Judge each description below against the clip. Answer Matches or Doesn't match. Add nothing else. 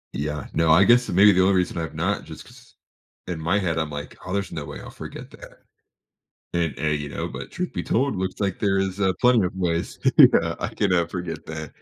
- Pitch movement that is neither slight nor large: Matches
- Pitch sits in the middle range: Doesn't match